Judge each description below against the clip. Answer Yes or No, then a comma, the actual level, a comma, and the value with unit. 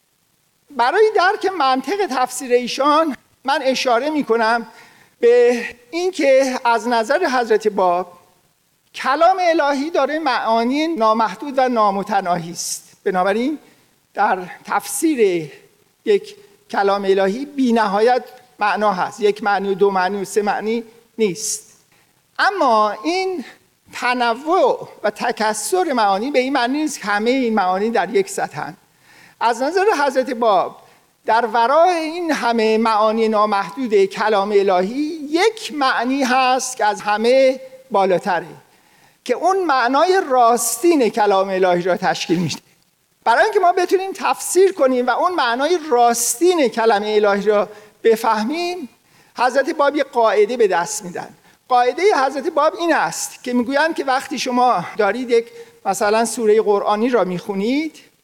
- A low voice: No, high, 245 Hz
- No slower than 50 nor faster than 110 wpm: No, average, 130 wpm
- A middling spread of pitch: No, wide, 5.9 semitones